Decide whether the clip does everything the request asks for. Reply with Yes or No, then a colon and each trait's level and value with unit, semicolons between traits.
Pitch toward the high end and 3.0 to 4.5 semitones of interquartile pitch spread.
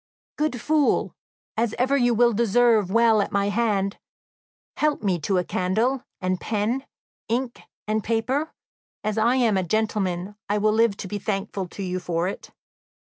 Yes: high, 215 Hz; average, 3.4 semitones